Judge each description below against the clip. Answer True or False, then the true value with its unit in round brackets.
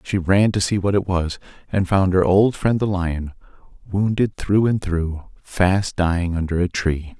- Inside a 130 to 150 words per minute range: False (190 wpm)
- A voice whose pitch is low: True (95 Hz)